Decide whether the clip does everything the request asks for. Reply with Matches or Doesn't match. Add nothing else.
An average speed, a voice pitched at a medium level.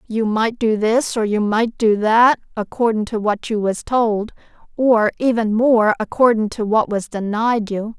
Doesn't match